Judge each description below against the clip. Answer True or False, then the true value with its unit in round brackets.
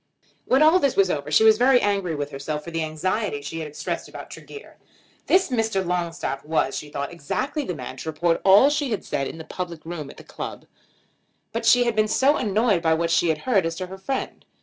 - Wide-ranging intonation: True (6.3 semitones)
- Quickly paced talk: True (225 wpm)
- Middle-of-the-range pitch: True (180 Hz)